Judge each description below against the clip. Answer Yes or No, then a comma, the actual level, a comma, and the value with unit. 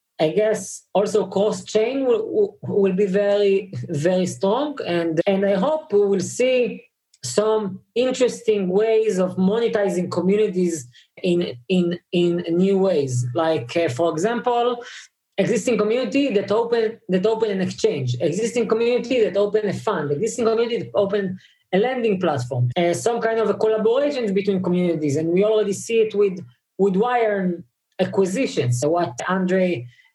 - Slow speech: No, average, 145 wpm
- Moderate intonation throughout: Yes, average, 3.9 semitones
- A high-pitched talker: Yes, high, 200 Hz